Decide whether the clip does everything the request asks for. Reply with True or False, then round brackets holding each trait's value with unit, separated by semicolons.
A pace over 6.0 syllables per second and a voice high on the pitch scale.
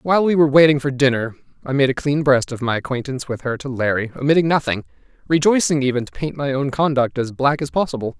False (6.5 syllables/s; 135 Hz)